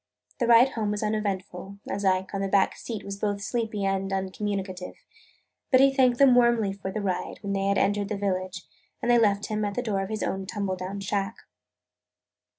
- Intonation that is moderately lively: No, narrow, 2.0 semitones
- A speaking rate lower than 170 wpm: No, fast, 205 wpm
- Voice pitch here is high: Yes, high, 200 Hz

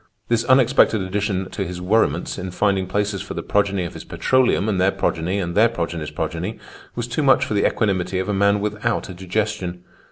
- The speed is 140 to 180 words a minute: No, average, 200 wpm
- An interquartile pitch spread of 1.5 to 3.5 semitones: Yes, average, 2.9 semitones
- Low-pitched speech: Yes, low, 100 Hz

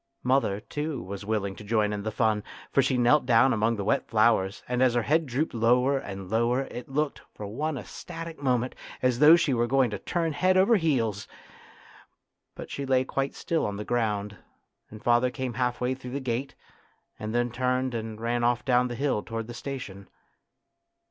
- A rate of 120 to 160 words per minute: No, average, 195 wpm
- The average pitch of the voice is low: Yes, low, 120 Hz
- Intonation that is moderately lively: Yes, average, 3.5 semitones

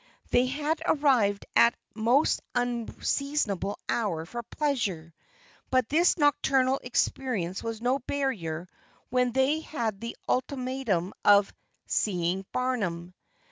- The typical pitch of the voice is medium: No, high, 245 Hz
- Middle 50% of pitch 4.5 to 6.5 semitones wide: Yes, average, 5.1 semitones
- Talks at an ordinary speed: No, slow, 110 wpm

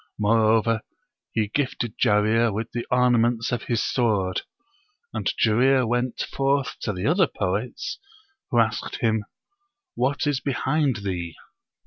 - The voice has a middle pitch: No, low, 115 Hz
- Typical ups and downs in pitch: Yes, average, 3.1 semitones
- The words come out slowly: Yes, slow, 125 wpm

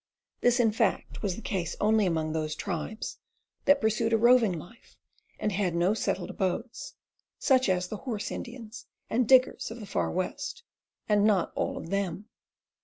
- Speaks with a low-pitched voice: No, high, 210 Hz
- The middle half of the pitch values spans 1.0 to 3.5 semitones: No, average, 4.2 semitones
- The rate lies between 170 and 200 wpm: Yes, average, 175 wpm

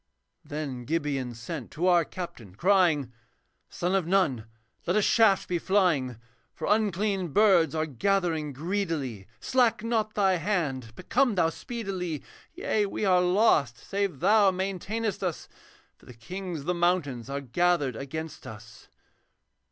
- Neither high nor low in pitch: Yes, medium, 175 Hz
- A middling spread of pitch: No, wide, 5.8 semitones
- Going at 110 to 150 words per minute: Yes, average, 145 wpm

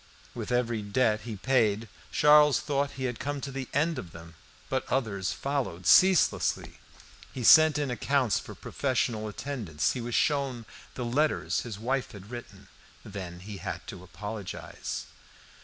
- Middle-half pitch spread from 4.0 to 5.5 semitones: Yes, average, 5.2 semitones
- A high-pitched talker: No, low, 120 Hz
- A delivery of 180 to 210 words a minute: No, average, 155 wpm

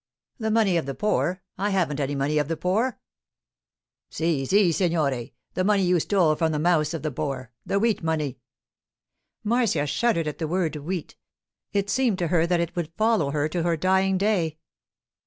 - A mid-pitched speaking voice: Yes, medium, 170 Hz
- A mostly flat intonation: No, average, 4.2 semitones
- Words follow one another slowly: No, average, 180 wpm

